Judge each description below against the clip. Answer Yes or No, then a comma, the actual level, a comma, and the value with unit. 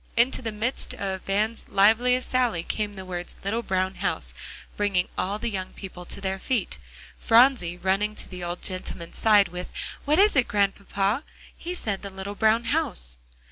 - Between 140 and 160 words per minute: No, average, 175 wpm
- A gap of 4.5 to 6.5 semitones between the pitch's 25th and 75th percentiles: No, average, 3.6 semitones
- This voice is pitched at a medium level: No, high, 205 Hz